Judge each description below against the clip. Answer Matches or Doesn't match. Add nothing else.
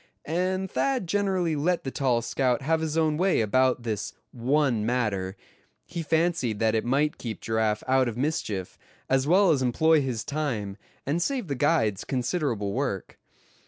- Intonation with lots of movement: Matches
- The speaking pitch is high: Doesn't match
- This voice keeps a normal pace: Matches